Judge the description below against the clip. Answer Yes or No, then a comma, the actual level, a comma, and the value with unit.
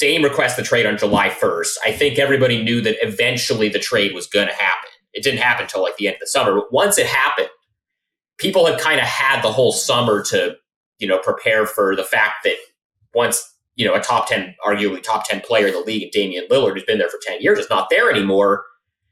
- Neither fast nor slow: No, fast, 230 wpm